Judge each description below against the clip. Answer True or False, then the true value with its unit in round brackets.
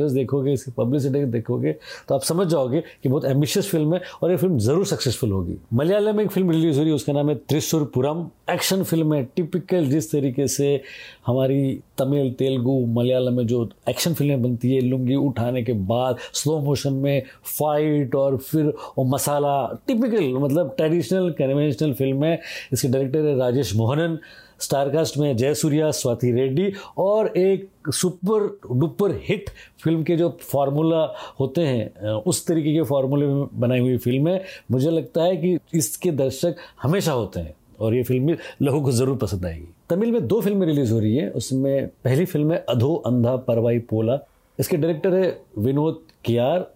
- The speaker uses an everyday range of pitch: True (4.4 semitones)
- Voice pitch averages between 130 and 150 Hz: True (140 Hz)